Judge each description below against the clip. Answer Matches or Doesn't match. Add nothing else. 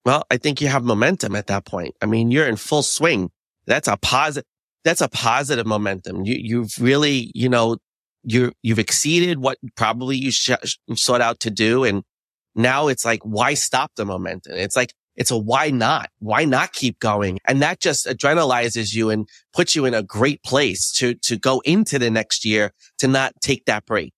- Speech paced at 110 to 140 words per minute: Doesn't match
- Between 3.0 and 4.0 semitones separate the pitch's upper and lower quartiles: Matches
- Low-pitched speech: Matches